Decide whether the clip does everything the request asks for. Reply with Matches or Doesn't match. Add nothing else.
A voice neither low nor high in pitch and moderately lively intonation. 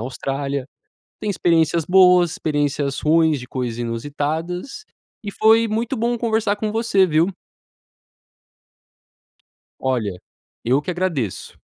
Doesn't match